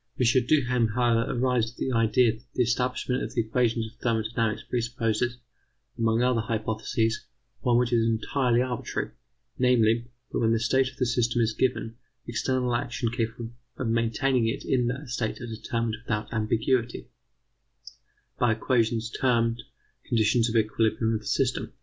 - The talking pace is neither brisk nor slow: Yes, average, 155 wpm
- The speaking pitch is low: Yes, low, 115 Hz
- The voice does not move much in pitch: Yes, narrow, 1.7 semitones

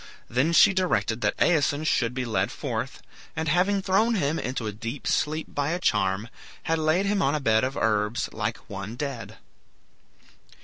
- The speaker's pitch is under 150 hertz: Yes, medium, 140 Hz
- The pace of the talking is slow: No, average, 175 wpm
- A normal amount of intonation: No, wide, 6.4 semitones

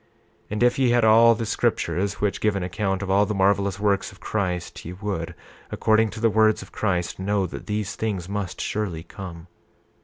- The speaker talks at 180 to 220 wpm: Yes, fast, 205 wpm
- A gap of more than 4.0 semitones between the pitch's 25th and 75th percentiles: No, narrow, 2.5 semitones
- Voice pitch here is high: No, low, 100 Hz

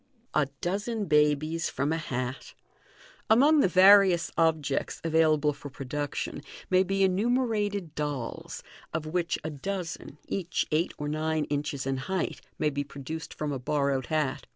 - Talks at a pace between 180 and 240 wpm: No, average, 150 wpm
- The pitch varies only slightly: No, average, 4.3 semitones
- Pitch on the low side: No, medium, 155 Hz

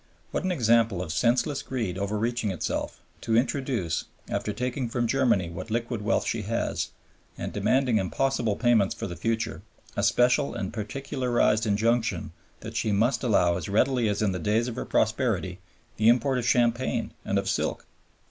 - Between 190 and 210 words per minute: No, average, 165 wpm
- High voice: No, low, 115 Hz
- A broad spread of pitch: No, average, 3.2 semitones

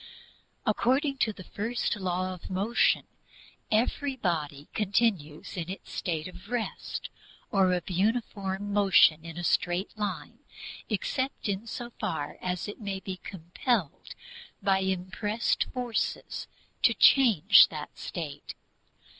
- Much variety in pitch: No, average, 3.9 semitones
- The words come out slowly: Yes, slow, 120 wpm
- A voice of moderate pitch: No, high, 195 Hz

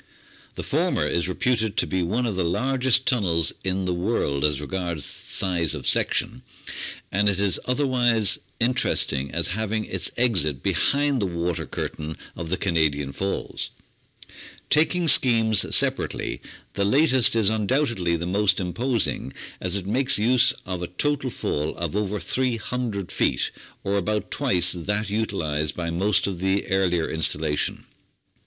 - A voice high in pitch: No, low, 100 Hz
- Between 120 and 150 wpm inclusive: Yes, average, 145 wpm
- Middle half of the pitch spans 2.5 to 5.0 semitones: No, wide, 5.4 semitones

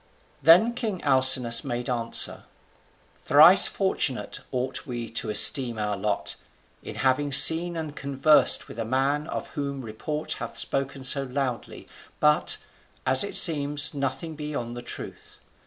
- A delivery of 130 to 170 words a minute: Yes, average, 140 wpm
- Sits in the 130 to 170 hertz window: Yes, low, 135 Hz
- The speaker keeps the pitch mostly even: No, average, 3.4 semitones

